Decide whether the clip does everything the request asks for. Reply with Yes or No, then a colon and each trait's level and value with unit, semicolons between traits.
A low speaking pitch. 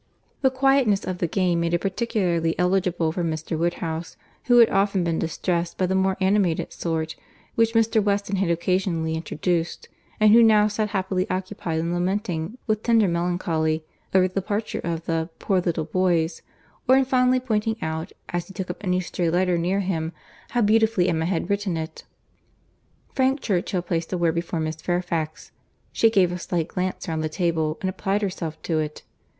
No: medium, 180 Hz